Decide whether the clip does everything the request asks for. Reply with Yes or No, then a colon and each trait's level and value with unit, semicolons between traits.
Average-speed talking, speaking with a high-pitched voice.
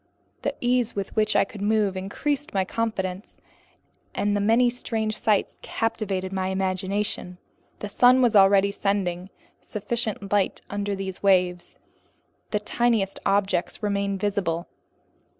No: slow, 130 wpm; high, 200 Hz